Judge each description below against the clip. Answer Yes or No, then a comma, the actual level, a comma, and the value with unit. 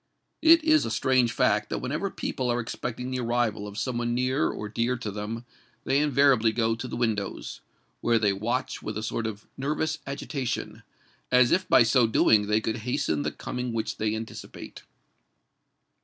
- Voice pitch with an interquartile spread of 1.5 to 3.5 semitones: Yes, narrow, 2.6 semitones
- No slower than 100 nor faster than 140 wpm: No, average, 175 wpm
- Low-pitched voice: Yes, low, 120 Hz